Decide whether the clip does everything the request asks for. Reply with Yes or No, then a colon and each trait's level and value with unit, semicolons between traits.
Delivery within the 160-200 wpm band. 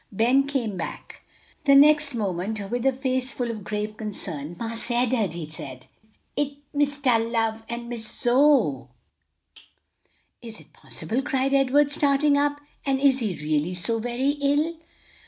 No: average, 145 wpm